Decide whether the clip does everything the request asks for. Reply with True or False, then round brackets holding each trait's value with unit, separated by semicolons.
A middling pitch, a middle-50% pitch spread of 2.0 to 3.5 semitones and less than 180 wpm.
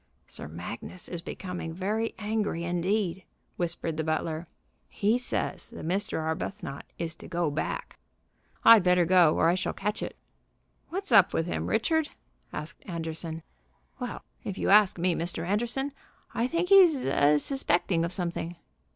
False (180 Hz; 4.5 semitones; 150 wpm)